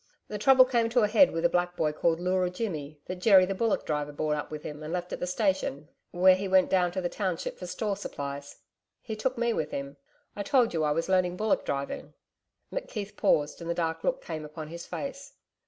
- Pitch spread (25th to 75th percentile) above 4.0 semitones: Yes, average, 5.2 semitones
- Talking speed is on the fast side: Yes, fast, 230 wpm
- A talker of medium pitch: Yes, medium, 180 Hz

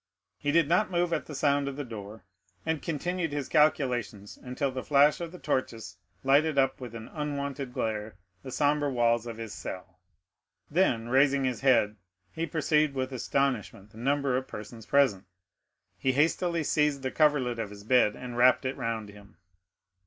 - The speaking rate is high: No, average, 175 wpm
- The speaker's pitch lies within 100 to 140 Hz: Yes, low, 135 Hz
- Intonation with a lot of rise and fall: No, average, 4.3 semitones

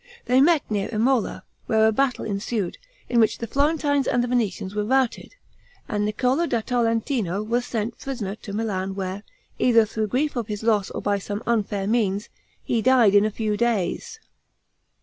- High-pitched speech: Yes, high, 225 Hz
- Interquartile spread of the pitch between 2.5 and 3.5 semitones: Yes, average, 3.2 semitones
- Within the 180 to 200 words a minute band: No, average, 170 wpm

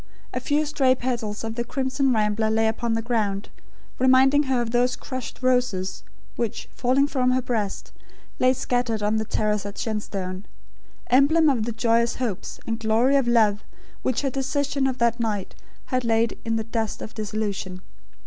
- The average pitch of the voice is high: Yes, high, 235 Hz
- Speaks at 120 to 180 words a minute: Yes, average, 170 wpm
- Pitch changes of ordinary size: Yes, average, 3.0 semitones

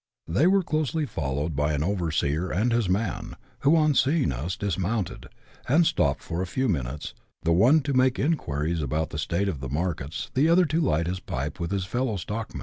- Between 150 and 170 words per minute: No, average, 200 wpm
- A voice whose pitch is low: Yes, very low, 95 Hz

